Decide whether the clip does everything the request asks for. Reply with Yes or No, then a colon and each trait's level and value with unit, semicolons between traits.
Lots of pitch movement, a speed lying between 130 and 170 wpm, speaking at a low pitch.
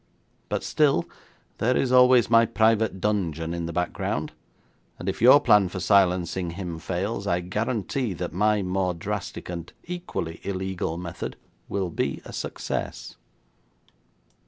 No: average, 4.1 semitones; slow, 135 wpm; very low, 95 Hz